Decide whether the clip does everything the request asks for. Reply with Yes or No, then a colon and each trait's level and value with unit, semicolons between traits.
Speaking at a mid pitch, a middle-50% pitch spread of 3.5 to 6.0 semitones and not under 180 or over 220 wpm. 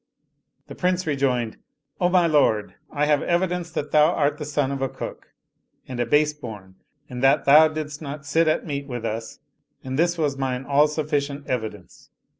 No: medium, 145 Hz; average, 2.9 semitones; average, 190 wpm